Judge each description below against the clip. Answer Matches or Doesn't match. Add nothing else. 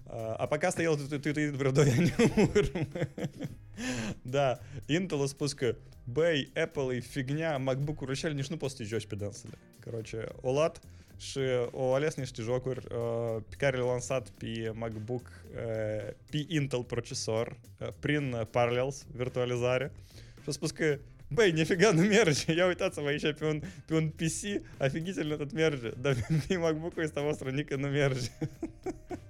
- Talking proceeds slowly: Matches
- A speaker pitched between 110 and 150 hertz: Matches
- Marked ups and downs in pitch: Doesn't match